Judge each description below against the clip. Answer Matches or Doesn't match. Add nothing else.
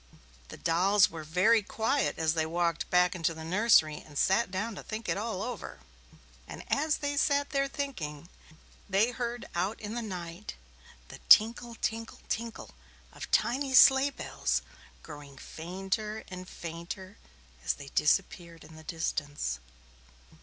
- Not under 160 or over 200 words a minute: Doesn't match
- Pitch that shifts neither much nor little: Doesn't match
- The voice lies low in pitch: Doesn't match